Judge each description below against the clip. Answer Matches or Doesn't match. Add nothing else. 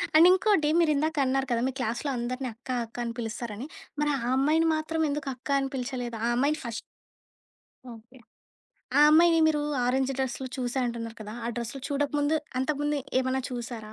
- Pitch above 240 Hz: Matches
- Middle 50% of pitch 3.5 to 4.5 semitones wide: Matches